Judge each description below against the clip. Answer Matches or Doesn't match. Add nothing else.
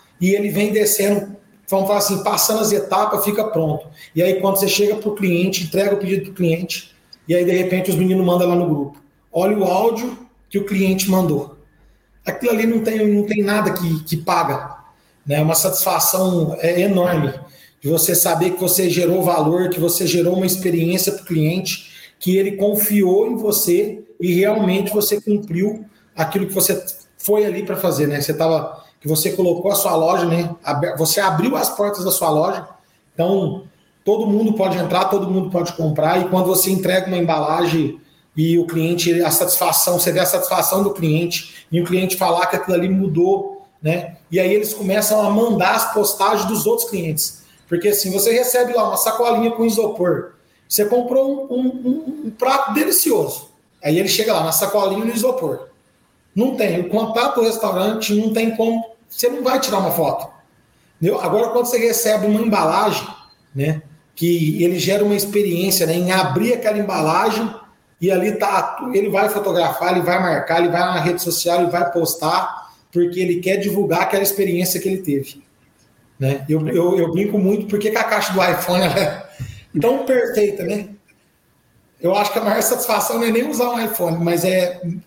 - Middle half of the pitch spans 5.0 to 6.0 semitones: Doesn't match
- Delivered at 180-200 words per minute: Matches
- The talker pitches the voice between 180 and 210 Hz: Matches